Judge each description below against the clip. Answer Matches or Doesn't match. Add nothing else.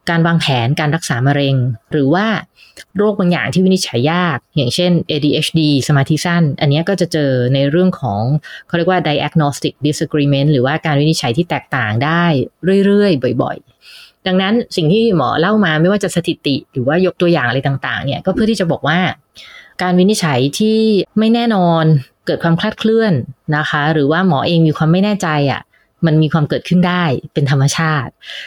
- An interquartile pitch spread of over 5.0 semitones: Doesn't match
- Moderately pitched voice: Matches